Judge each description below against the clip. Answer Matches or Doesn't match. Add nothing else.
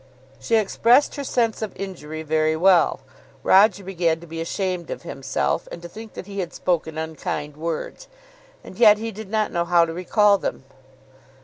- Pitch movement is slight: Doesn't match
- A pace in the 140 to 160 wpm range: Doesn't match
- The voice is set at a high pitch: Doesn't match